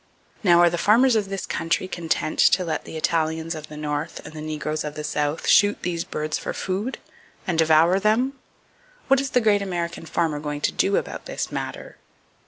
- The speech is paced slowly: No, average, 195 wpm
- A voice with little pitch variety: No, average, 4.1 semitones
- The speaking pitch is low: No, medium, 170 Hz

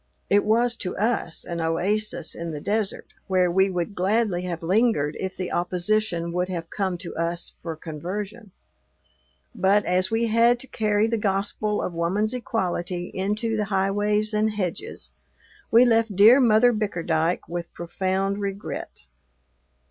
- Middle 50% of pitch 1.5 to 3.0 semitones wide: No, average, 3.5 semitones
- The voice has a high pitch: Yes, high, 195 Hz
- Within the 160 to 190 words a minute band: No, average, 150 wpm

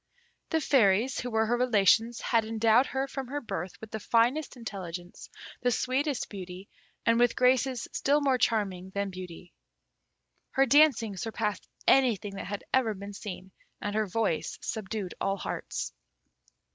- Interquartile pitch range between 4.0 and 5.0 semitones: Yes, average, 4.3 semitones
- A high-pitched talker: Yes, high, 225 Hz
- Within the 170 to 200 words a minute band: No, average, 150 wpm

